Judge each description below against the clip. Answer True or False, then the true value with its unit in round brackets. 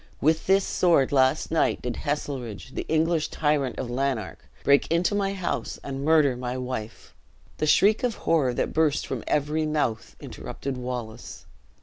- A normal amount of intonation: True (4.0 semitones)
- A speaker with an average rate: True (155 wpm)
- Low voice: False (145 Hz)